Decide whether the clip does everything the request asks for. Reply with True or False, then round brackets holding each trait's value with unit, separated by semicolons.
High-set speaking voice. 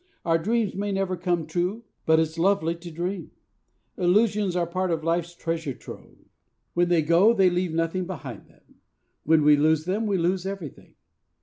False (175 Hz)